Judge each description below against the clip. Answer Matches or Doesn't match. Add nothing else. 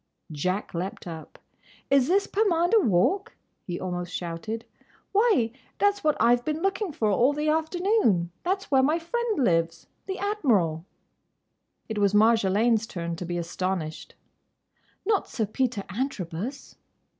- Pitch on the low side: Doesn't match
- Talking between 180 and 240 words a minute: Doesn't match